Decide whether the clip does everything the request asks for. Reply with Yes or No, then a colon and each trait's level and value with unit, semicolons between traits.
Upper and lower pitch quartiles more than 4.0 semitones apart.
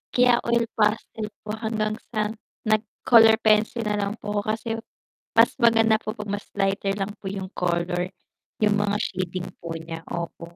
No: narrow, 2.4 semitones